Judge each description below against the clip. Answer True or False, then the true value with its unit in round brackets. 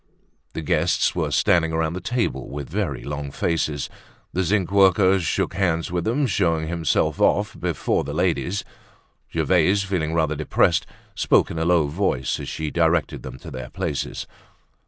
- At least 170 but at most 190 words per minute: False (160 wpm)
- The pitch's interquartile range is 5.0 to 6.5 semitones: False (3.3 semitones)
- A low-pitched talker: True (85 Hz)